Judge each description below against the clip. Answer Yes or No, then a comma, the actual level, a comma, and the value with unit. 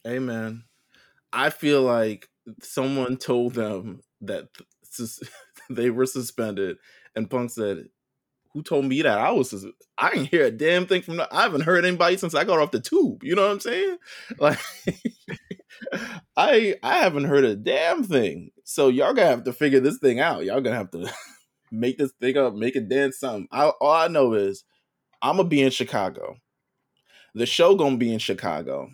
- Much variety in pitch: Yes, wide, 6.2 semitones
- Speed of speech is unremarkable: Yes, average, 185 wpm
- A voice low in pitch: Yes, low, 130 Hz